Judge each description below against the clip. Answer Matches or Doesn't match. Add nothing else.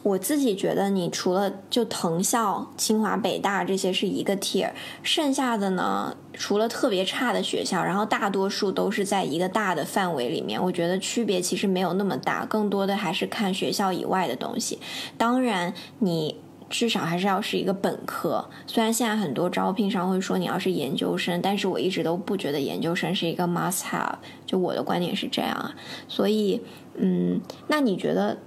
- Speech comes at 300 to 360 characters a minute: Matches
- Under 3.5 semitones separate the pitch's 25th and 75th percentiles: Matches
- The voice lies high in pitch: Matches